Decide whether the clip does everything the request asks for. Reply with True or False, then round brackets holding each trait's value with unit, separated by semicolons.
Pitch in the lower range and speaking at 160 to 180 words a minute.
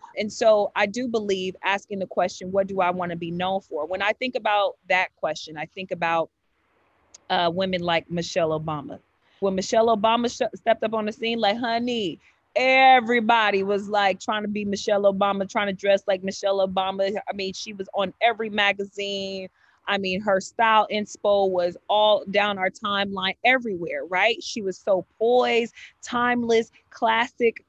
False (200 Hz; 175 wpm)